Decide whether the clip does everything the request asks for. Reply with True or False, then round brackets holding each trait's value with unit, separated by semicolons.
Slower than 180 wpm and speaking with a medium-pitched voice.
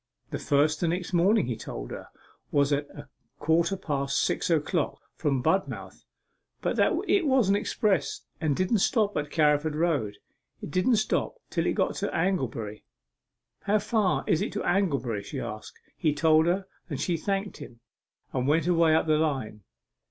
True (170 wpm; 160 Hz)